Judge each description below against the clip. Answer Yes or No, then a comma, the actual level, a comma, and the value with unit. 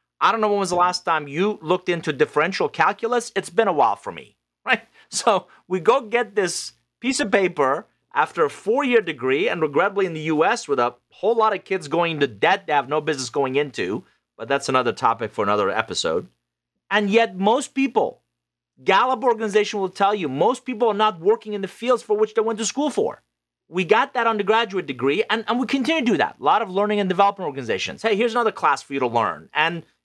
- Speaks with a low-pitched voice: No, high, 200 Hz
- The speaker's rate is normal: No, fast, 225 wpm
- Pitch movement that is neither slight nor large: No, wide, 6.9 semitones